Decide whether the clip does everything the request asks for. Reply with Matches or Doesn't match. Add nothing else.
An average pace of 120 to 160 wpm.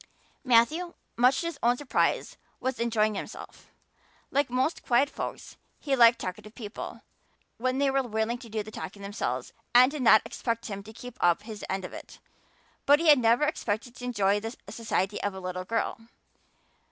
Doesn't match